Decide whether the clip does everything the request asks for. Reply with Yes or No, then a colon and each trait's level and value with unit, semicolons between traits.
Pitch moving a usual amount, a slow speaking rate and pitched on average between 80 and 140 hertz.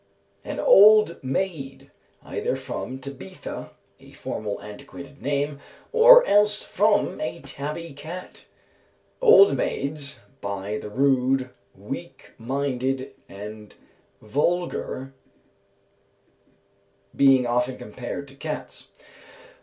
Yes: average, 4.0 semitones; slow, 95 wpm; low, 135 Hz